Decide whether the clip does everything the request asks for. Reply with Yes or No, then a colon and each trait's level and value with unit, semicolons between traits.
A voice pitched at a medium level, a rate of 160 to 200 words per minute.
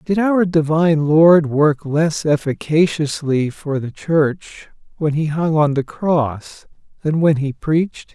No: medium, 155 Hz; average, 145 wpm